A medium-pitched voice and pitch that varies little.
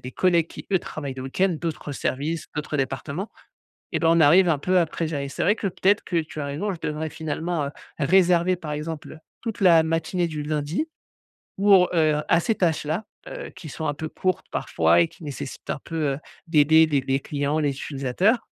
No: medium, 160 Hz; average, 3.5 semitones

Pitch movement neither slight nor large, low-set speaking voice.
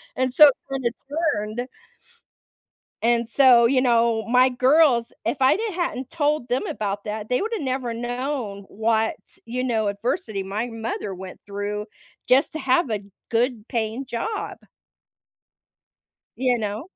No: average, 3.3 semitones; high, 240 Hz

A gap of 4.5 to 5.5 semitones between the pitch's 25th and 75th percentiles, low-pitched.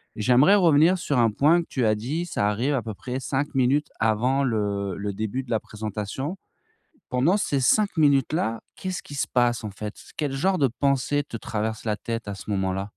Yes: average, 5.2 semitones; low, 125 Hz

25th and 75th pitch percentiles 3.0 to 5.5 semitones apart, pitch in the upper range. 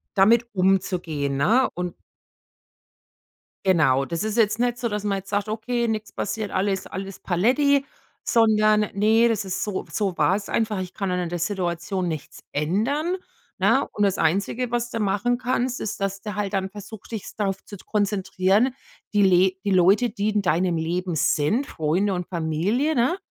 Yes: average, 3.4 semitones; high, 200 Hz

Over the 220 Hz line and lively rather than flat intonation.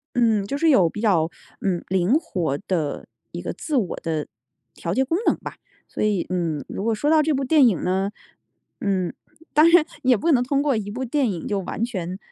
No: high, 210 Hz; wide, 6.7 semitones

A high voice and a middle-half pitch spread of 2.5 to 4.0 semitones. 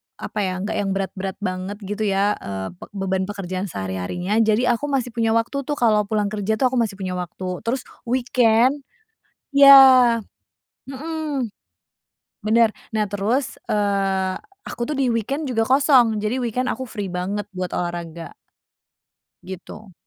No: high, 215 Hz; average, 4.7 semitones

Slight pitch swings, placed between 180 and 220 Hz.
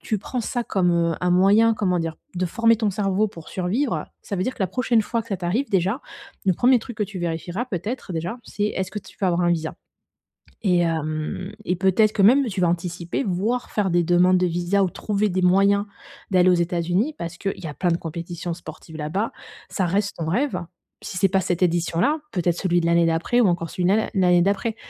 No: average, 3.3 semitones; medium, 185 Hz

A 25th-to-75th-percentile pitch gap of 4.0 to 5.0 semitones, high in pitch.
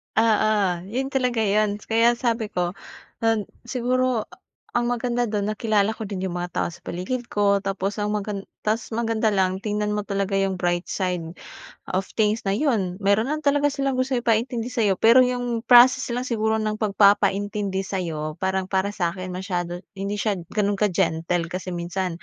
No: average, 3.5 semitones; high, 210 Hz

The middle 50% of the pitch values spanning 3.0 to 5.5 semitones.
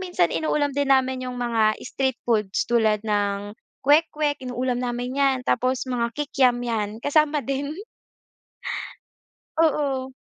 Yes: average, 3.3 semitones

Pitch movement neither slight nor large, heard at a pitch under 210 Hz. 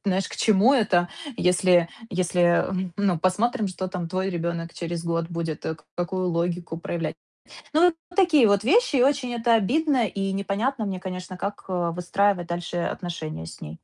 Yes: average, 3.5 semitones; medium, 185 Hz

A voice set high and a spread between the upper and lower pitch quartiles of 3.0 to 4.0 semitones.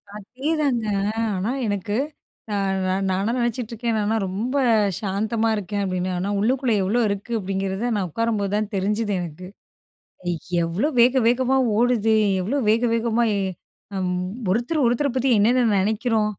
Yes: high, 220 Hz; average, 3.5 semitones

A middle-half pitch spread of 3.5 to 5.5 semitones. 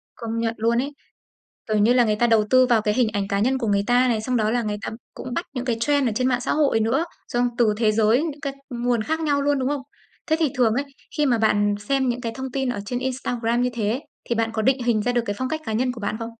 No: average, 2.9 semitones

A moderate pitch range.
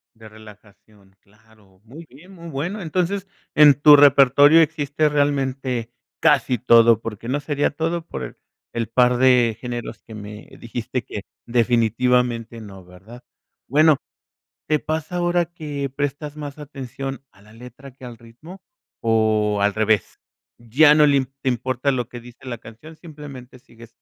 Yes: average, 4.4 semitones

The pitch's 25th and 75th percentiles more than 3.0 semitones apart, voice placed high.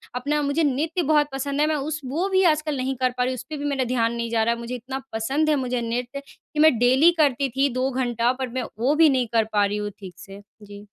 Yes: average, 3.9 semitones; very high, 260 Hz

